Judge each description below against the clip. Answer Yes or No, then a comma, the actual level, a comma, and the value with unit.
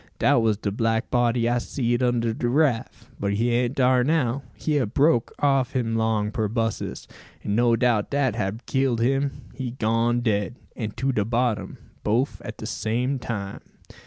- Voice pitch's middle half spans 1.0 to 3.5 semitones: Yes, narrow, 2.4 semitones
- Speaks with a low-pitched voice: Yes, low, 120 Hz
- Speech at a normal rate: Yes, average, 175 wpm